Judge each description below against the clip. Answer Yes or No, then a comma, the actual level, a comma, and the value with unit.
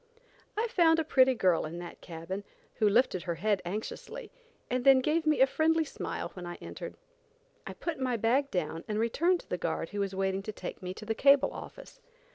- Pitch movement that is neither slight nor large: No, wide, 8.2 semitones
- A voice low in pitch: No, high, 225 Hz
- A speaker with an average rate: No, fast, 210 wpm